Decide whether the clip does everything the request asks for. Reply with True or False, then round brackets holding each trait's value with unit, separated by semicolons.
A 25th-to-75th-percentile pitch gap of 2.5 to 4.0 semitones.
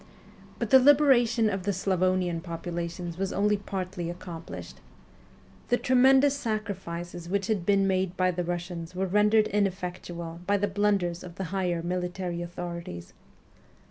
True (2.8 semitones)